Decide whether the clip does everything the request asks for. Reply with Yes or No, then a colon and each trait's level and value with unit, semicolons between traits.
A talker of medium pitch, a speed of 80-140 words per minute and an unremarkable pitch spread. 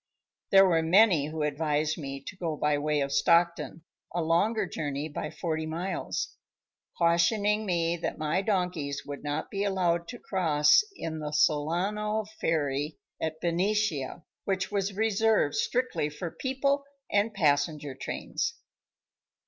Yes: medium, 170 Hz; slow, 135 wpm; average, 4.7 semitones